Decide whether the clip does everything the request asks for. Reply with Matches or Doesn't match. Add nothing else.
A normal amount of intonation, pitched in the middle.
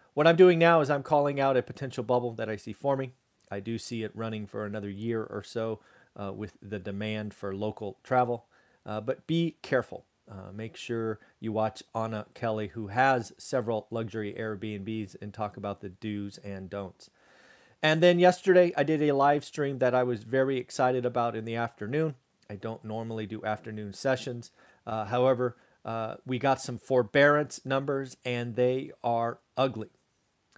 Doesn't match